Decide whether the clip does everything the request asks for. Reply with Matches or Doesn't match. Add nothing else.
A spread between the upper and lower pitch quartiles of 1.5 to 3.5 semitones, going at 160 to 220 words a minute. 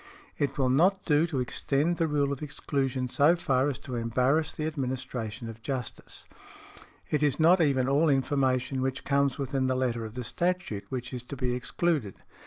Matches